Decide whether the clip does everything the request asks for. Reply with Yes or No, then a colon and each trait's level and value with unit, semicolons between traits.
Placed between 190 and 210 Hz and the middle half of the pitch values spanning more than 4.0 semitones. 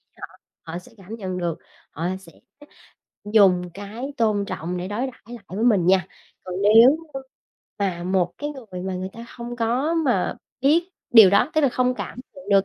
Yes: high, 205 Hz; average, 5.1 semitones